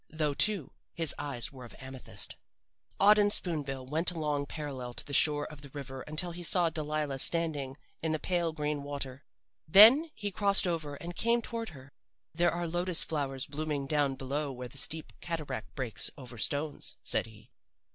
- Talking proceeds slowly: No, average, 175 wpm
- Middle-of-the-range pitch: Yes, medium, 150 Hz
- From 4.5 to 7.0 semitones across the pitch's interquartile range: No, average, 3.7 semitones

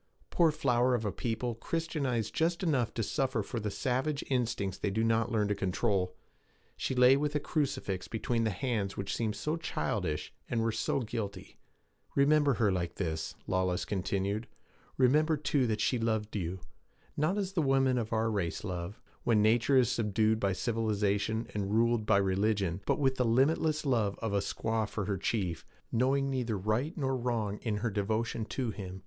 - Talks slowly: No, average, 180 wpm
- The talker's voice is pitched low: Yes, low, 115 Hz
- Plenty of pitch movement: No, average, 4.4 semitones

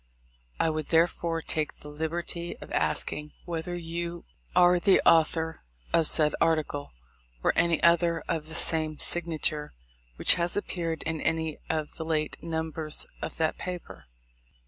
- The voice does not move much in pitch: Yes, narrow, 1.5 semitones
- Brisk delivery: No, average, 145 wpm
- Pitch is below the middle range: No, medium, 160 Hz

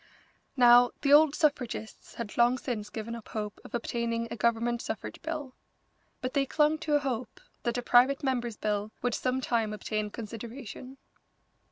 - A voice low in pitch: No, high, 240 Hz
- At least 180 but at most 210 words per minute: No, average, 165 wpm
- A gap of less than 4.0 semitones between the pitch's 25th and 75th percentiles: Yes, average, 2.8 semitones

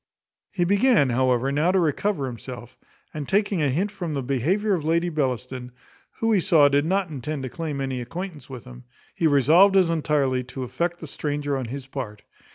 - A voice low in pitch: No, medium, 145 Hz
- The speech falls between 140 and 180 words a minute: No, average, 190 wpm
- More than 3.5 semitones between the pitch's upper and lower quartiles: Yes, average, 5.1 semitones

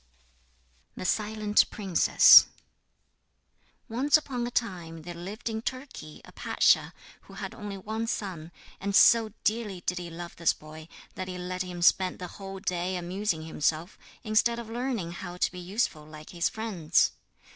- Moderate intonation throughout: Yes, average, 4.1 semitones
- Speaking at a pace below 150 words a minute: No, average, 155 wpm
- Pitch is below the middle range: No, medium, 185 Hz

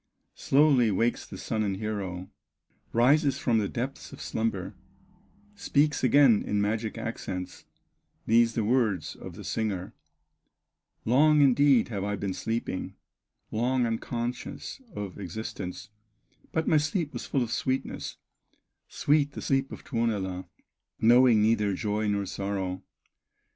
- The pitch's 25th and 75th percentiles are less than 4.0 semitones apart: No, average, 4.4 semitones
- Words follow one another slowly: Yes, slow, 130 wpm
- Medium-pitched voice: No, low, 115 Hz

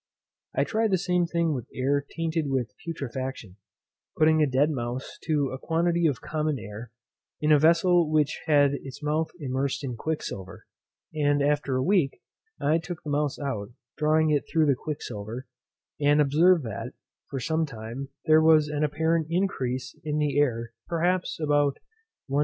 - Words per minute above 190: No, average, 165 wpm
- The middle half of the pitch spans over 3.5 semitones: No, average, 3.2 semitones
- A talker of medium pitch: Yes, medium, 150 Hz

